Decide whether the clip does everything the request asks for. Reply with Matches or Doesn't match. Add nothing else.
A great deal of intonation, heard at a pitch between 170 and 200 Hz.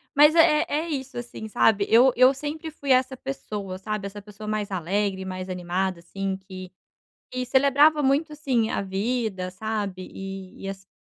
Doesn't match